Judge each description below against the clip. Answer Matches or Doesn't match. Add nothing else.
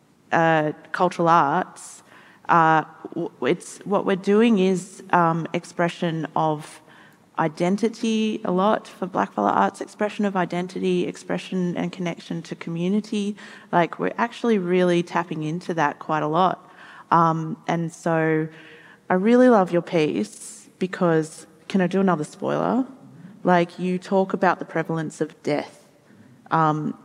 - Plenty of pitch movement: Doesn't match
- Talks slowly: Matches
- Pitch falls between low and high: Matches